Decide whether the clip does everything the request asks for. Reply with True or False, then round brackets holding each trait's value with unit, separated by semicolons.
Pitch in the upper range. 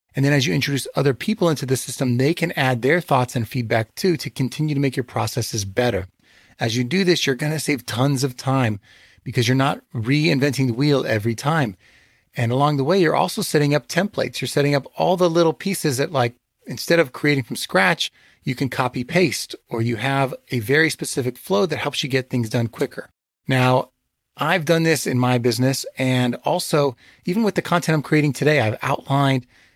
False (135 Hz)